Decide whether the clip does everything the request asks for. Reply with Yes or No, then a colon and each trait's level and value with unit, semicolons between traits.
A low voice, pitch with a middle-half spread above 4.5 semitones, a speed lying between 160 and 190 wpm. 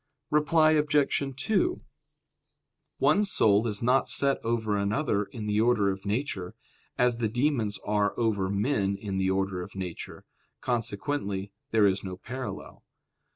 No: low, 110 Hz; average, 5.1 semitones; average, 140 wpm